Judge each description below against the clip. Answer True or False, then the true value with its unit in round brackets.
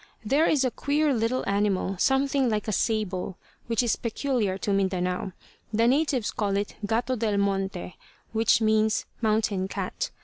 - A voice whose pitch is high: True (220 Hz)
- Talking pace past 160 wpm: False (150 wpm)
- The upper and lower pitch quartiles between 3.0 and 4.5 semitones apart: True (4.1 semitones)